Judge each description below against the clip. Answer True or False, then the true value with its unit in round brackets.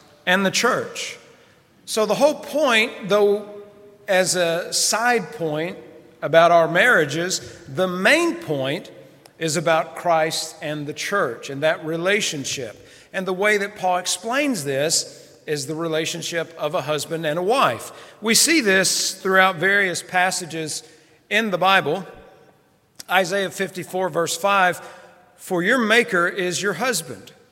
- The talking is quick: False (135 wpm)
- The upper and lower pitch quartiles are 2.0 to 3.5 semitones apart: False (4.0 semitones)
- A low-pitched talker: False (180 Hz)